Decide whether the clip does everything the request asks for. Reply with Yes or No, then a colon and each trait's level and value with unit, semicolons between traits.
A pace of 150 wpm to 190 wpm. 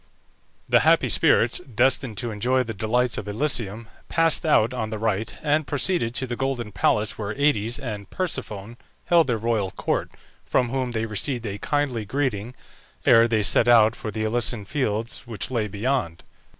Yes: average, 170 wpm